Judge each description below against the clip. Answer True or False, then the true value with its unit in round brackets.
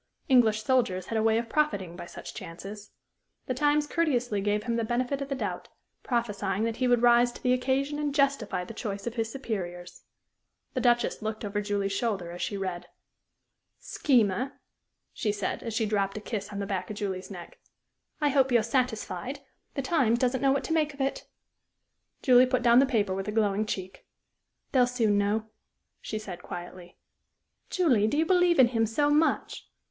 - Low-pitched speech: False (225 Hz)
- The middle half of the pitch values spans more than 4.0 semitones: True (4.4 semitones)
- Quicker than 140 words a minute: True (190 wpm)